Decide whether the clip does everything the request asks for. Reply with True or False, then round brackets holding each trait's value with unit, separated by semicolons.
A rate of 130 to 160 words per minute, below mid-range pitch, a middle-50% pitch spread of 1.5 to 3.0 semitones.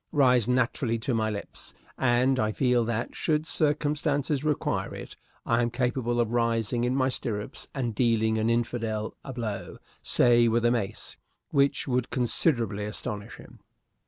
True (155 wpm; 120 Hz; 2.5 semitones)